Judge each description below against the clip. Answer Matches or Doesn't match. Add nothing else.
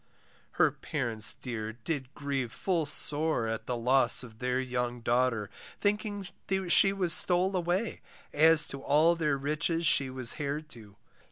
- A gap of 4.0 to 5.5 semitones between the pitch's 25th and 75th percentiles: Matches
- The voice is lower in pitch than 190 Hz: Matches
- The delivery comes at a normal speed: Matches